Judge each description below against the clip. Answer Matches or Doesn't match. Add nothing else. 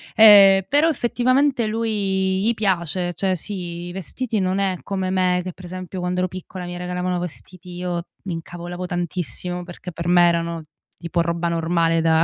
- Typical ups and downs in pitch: Doesn't match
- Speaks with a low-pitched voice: Doesn't match